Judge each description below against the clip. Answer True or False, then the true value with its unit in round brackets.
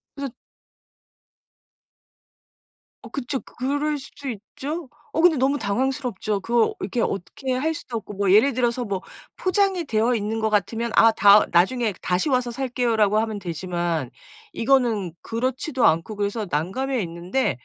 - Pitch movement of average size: True (4.9 semitones)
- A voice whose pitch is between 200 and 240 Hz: True (230 Hz)